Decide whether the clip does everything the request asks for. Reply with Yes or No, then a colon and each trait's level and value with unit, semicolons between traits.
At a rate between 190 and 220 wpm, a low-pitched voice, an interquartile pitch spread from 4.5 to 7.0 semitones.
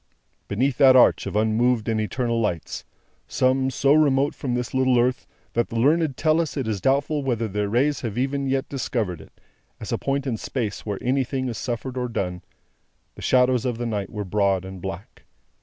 No: average, 195 wpm; low, 125 Hz; average, 3.7 semitones